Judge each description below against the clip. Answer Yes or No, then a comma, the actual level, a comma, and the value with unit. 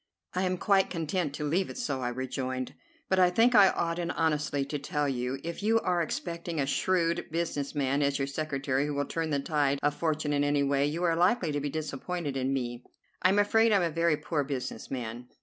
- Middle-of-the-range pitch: Yes, medium, 150 Hz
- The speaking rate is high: Yes, fast, 230 wpm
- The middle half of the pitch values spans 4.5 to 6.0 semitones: No, average, 4.0 semitones